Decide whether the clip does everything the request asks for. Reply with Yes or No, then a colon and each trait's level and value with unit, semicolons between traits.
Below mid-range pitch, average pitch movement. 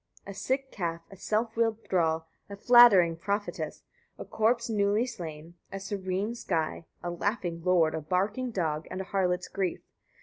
No: high, 195 Hz; average, 4.2 semitones